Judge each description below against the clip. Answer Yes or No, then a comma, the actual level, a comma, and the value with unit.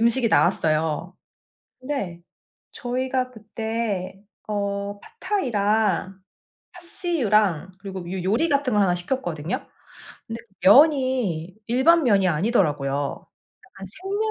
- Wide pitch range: Yes, wide, 5.7 semitones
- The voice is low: No, high, 210 Hz